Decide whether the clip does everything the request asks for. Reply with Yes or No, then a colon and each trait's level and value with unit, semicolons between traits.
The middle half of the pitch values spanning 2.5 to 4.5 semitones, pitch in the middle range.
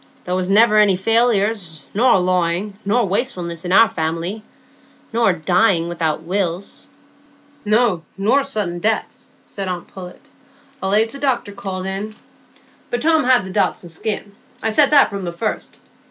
No: average, 3.9 semitones; high, 195 Hz